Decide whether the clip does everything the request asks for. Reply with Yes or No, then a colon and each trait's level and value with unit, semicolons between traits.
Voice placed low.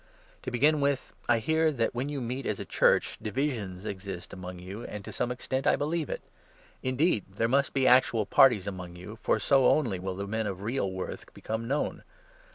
Yes: low, 115 Hz